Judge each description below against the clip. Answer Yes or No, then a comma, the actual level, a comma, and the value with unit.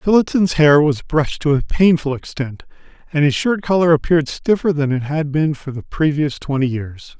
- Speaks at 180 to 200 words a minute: Yes, average, 190 wpm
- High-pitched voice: No, medium, 150 Hz